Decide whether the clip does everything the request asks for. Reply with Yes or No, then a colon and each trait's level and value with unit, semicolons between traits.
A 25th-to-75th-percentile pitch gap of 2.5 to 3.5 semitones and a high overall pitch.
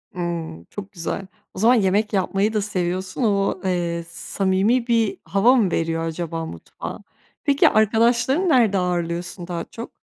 No: average, 4.4 semitones; high, 195 Hz